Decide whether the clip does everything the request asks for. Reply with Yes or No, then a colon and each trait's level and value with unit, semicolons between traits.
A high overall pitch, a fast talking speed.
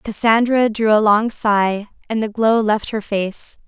No: high, 215 Hz; average, 180 wpm